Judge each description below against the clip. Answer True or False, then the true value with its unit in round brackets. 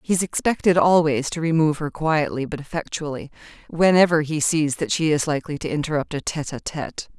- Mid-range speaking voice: True (155 Hz)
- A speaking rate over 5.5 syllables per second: True (5.9 syllables/s)